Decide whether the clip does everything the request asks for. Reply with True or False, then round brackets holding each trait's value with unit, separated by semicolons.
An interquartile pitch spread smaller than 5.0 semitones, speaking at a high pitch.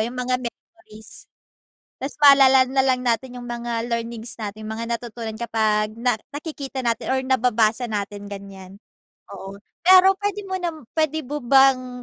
True (3.6 semitones; 240 Hz)